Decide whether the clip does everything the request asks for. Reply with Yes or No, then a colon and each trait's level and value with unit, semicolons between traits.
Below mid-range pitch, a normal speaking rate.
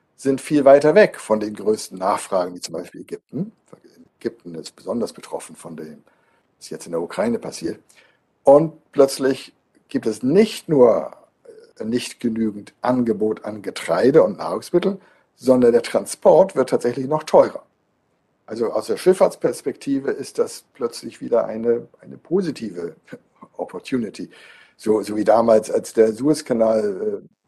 Yes: low, 130 Hz; average, 140 wpm